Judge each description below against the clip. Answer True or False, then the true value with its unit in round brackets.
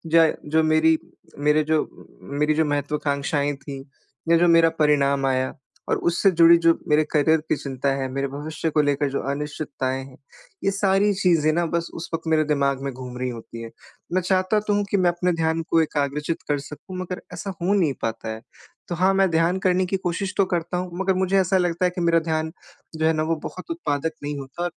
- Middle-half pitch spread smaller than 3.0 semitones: False (3.8 semitones)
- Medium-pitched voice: True (160 Hz)